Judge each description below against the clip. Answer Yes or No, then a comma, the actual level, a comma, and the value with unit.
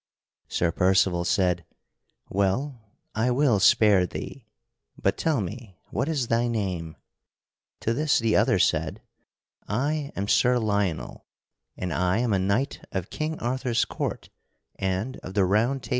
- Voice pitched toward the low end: Yes, low, 110 Hz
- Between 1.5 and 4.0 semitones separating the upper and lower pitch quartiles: No, average, 4.9 semitones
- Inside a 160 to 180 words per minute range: No, average, 145 wpm